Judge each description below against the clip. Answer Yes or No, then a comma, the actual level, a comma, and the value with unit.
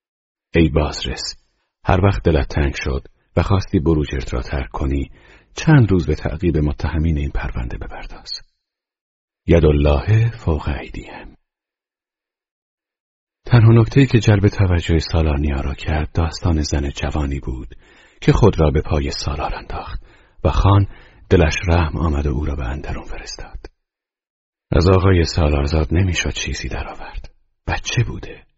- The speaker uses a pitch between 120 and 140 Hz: No, very low, 80 Hz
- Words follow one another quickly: No, average, 135 wpm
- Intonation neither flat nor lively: Yes, average, 4.5 semitones